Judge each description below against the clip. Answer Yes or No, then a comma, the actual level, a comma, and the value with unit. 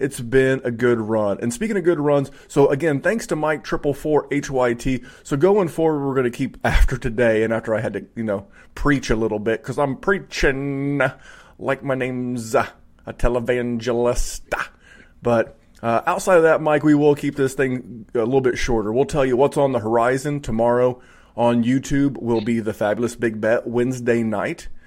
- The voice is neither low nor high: No, low, 130 Hz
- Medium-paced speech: Yes, average, 190 wpm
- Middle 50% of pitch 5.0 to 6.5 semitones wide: No, average, 3.3 semitones